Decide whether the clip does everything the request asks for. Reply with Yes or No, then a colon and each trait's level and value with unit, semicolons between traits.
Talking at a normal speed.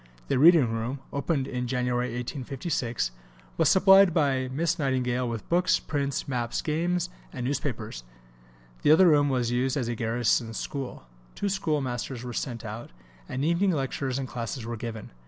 Yes: average, 155 wpm